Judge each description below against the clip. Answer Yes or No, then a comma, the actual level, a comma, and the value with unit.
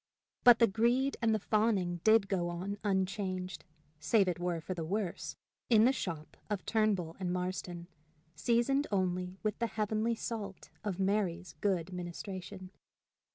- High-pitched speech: Yes, high, 195 Hz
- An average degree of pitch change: Yes, average, 3.3 semitones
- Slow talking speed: No, average, 150 wpm